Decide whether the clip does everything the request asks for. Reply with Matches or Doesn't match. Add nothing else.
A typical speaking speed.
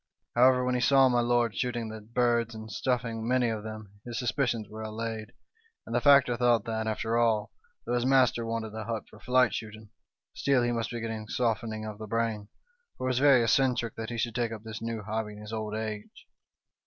Doesn't match